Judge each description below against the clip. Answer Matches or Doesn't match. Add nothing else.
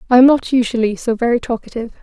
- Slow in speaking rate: Doesn't match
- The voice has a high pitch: Matches